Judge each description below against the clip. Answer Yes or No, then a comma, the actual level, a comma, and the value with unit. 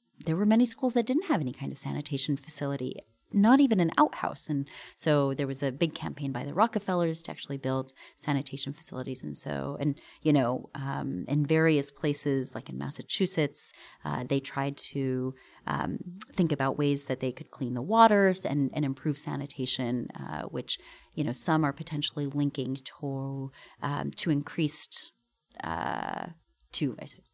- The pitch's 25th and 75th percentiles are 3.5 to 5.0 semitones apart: No, average, 3.0 semitones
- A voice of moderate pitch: Yes, medium, 145 Hz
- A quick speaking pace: No, average, 170 wpm